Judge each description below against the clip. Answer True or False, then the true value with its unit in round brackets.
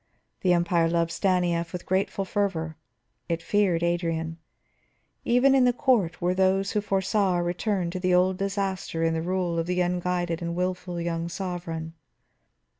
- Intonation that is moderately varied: False (2.2 semitones)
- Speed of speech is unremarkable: True (155 wpm)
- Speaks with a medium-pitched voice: True (180 Hz)